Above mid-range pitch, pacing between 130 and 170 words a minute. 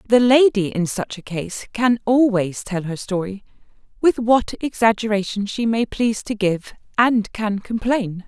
Yes: high, 215 Hz; average, 160 wpm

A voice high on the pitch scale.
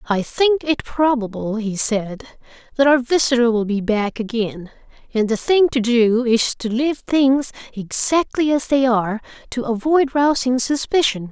Yes: high, 245 Hz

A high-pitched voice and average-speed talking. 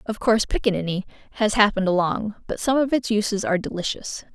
Yes: high, 210 Hz; average, 180 wpm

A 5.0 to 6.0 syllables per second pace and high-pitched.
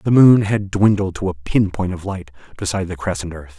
No: 5.5 syllables/s; very low, 95 Hz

